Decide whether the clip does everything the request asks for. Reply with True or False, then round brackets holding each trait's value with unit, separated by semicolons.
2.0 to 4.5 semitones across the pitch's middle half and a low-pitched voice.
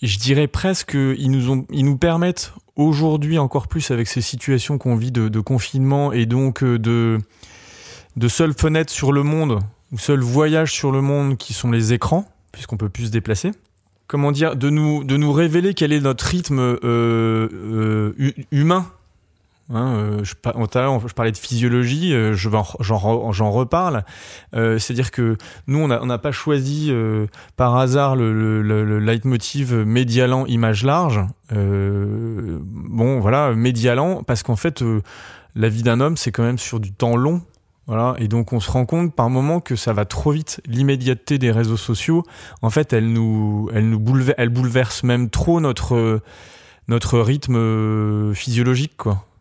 True (3.9 semitones; 120 Hz)